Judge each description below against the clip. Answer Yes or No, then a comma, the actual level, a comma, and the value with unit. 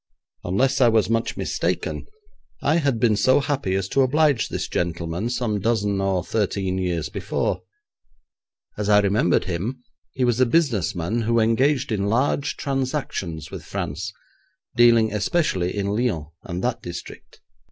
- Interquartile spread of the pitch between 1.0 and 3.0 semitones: No, average, 5.2 semitones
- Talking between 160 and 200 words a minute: No, average, 150 wpm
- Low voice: Yes, low, 110 Hz